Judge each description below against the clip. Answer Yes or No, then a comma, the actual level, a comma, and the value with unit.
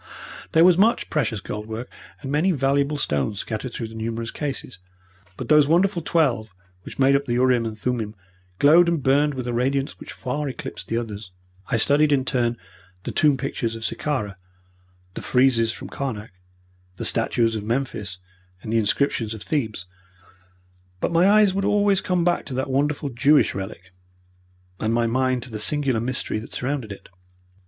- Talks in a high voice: No, low, 130 Hz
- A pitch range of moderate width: Yes, average, 4.6 semitones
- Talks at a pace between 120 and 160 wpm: No, average, 175 wpm